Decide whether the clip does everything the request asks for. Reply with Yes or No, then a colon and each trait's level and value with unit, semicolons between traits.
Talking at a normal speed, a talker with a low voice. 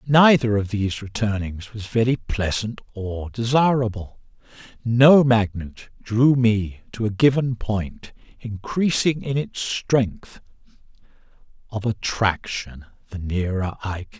No: slow, 115 wpm; low, 110 Hz